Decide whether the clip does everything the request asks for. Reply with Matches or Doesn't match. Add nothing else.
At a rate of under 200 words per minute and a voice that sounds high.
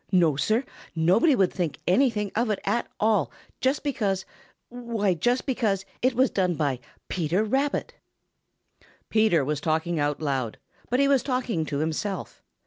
Matches